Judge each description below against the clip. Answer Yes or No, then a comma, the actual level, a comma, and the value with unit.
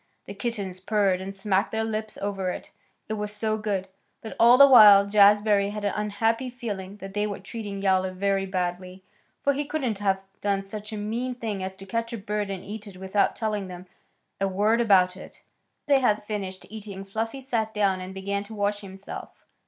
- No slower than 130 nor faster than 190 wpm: No, average, 200 wpm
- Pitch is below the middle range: No, high, 205 Hz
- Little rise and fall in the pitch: Yes, narrow, 2.2 semitones